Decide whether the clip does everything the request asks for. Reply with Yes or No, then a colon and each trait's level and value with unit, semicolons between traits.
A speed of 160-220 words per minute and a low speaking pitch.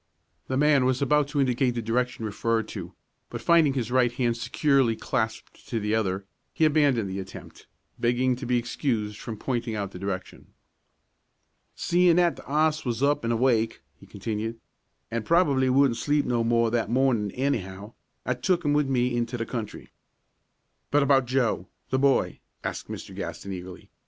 Yes: average, 170 wpm; low, 120 Hz